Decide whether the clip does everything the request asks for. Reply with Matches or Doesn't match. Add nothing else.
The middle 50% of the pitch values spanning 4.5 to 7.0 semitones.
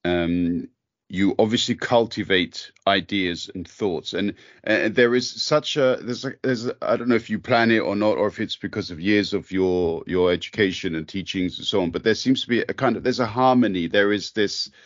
Matches